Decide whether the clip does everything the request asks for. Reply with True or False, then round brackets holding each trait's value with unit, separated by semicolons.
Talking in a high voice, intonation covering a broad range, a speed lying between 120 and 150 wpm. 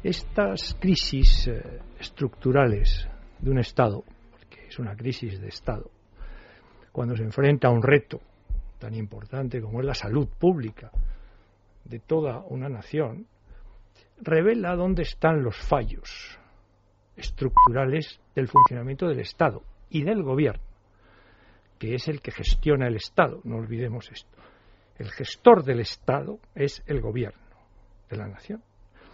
False (125 Hz; 5.9 semitones; 130 wpm)